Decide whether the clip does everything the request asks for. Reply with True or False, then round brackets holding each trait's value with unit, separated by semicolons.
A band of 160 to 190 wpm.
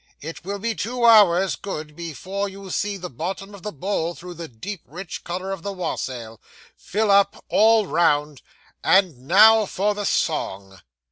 True (165 wpm)